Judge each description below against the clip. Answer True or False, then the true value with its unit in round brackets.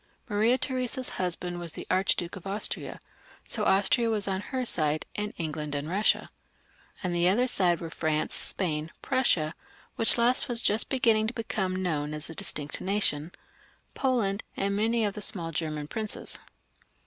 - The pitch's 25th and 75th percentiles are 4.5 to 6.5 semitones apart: True (5.1 semitones)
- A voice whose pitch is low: False (190 Hz)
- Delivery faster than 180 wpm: False (165 wpm)